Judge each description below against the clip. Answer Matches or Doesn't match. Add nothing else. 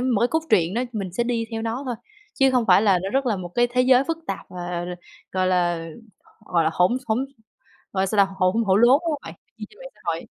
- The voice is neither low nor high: Doesn't match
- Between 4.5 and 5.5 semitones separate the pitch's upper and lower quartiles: Matches